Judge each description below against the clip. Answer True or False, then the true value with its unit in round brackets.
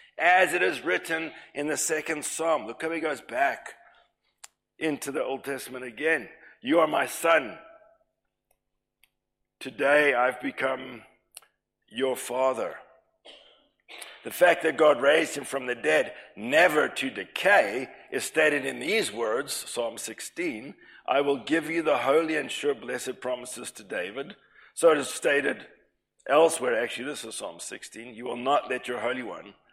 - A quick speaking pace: False (150 wpm)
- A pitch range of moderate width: True (3.5 semitones)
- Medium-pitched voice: True (145 Hz)